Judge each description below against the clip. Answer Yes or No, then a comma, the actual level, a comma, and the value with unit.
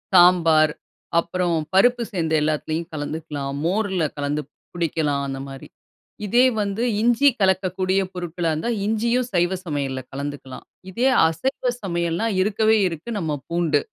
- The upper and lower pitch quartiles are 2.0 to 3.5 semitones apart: No, average, 4.5 semitones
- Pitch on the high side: No, medium, 170 Hz